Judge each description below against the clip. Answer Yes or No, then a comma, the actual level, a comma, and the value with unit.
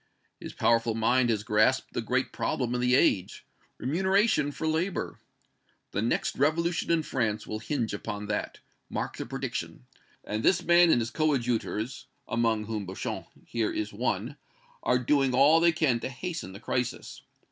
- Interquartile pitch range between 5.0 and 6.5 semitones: Yes, wide, 5.5 semitones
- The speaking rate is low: No, average, 160 wpm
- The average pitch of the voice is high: No, low, 125 Hz